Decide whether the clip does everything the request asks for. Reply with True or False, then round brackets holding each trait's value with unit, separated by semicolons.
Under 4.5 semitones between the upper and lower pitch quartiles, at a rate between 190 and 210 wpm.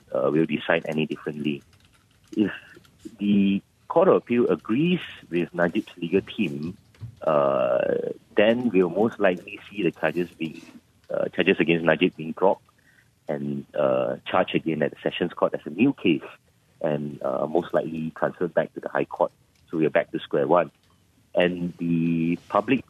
False (3.7 semitones; 160 wpm)